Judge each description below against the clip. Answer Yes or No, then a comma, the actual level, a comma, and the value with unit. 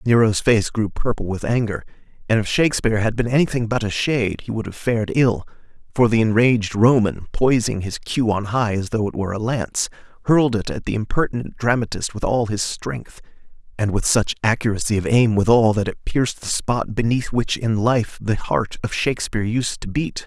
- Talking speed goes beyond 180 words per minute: Yes, average, 200 wpm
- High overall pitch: No, low, 110 Hz